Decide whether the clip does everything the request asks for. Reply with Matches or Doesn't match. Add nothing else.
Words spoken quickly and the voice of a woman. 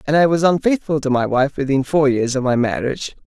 Doesn't match